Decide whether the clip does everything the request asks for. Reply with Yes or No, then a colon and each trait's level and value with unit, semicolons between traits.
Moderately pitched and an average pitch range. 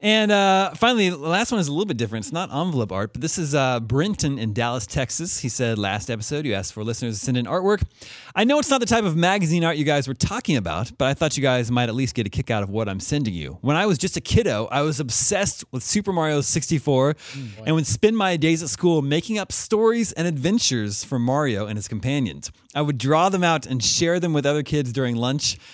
No: medium, 145 Hz; wide, 6.2 semitones